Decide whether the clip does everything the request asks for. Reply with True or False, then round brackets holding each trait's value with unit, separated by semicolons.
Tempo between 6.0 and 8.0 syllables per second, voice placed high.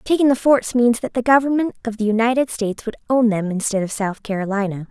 True (6.1 syllables/s; 230 Hz)